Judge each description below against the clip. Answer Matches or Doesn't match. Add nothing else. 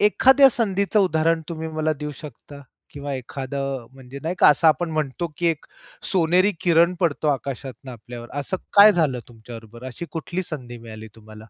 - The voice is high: Doesn't match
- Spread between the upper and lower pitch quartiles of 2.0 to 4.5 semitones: Doesn't match